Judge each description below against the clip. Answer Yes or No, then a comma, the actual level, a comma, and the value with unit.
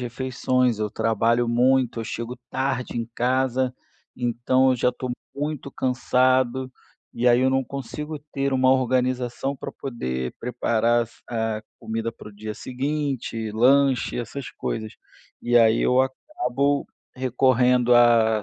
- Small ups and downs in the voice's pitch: Yes, narrow, 2.1 semitones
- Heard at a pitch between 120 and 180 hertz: Yes, low, 125 Hz